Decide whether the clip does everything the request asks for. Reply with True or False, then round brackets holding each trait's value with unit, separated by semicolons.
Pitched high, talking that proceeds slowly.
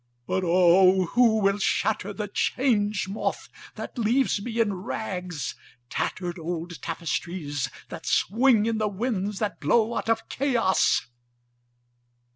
True (200 Hz; 120 wpm)